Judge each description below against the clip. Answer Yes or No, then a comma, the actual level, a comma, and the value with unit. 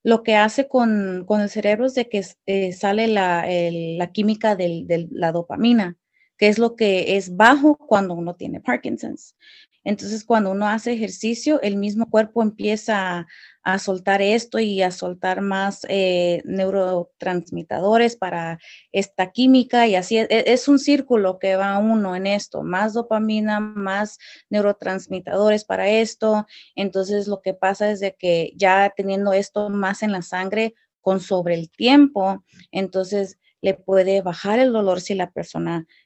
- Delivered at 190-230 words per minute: No, average, 160 wpm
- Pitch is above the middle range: Yes, high, 200 Hz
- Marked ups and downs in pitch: No, average, 2.7 semitones